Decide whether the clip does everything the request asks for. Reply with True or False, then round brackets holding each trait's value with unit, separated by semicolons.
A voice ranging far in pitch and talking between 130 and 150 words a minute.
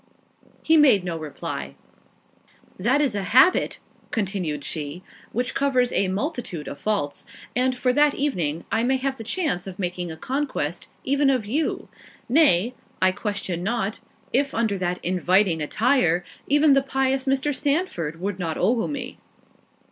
True (7.2 semitones; 145 wpm)